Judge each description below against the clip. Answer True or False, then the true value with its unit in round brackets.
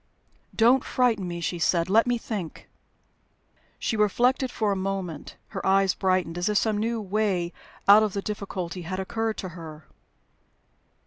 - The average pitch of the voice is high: True (195 Hz)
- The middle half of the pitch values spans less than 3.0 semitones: False (3.5 semitones)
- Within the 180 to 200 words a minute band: False (155 wpm)